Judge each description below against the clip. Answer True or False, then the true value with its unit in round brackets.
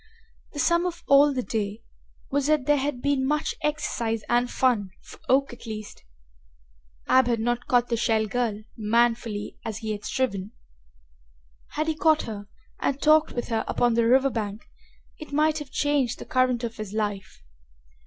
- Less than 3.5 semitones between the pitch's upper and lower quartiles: False (4.4 semitones)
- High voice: True (245 Hz)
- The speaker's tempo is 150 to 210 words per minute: True (175 wpm)